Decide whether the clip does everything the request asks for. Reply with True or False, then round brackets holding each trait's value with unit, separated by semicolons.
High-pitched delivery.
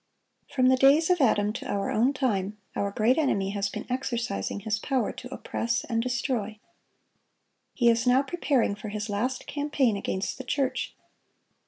True (240 Hz)